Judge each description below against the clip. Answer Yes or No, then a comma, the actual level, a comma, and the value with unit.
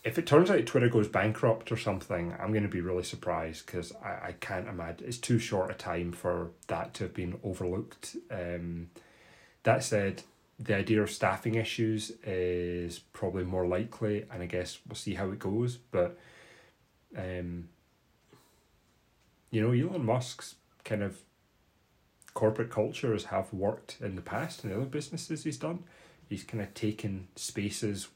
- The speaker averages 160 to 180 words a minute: Yes, average, 165 wpm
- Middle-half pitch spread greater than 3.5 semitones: Yes, average, 4.2 semitones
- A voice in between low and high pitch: No, low, 105 Hz